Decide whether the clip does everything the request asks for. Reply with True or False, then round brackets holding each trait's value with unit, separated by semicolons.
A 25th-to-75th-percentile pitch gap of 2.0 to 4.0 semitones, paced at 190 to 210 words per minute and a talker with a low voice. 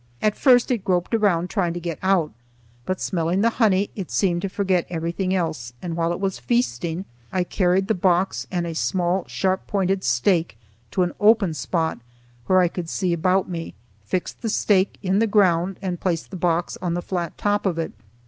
False (2.4 semitones; 195 wpm; 180 Hz)